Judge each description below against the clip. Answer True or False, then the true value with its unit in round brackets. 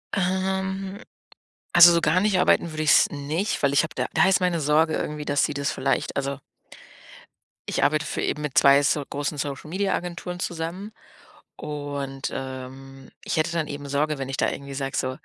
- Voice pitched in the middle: True (150 Hz)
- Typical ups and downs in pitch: True (3.9 semitones)